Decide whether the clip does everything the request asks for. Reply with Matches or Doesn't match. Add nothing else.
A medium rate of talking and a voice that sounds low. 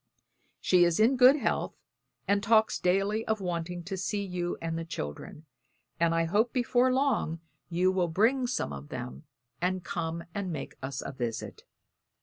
Doesn't match